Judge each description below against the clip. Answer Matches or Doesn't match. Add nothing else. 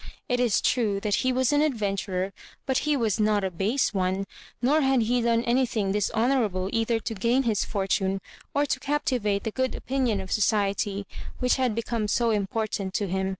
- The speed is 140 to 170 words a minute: Doesn't match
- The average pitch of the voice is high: Matches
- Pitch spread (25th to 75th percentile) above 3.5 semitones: Matches